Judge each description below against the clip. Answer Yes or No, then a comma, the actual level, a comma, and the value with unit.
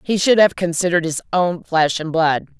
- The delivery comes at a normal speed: No, fast, 210 wpm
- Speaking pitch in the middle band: Yes, medium, 170 Hz